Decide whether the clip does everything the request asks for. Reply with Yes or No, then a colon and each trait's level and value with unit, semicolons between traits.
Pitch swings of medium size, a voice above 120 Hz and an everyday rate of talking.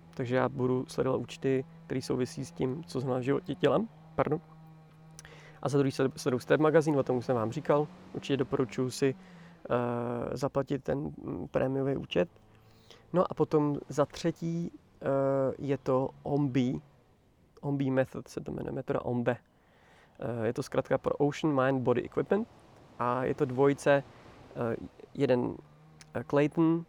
Yes: average, 3.3 semitones; medium, 140 Hz; average, 150 wpm